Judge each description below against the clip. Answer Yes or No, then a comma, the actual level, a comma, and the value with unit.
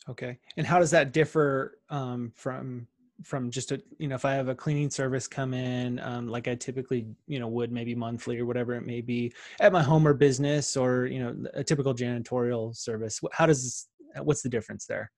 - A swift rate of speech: Yes, fast, 215 wpm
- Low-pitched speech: Yes, low, 130 Hz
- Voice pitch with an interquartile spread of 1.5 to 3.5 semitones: Yes, average, 3.0 semitones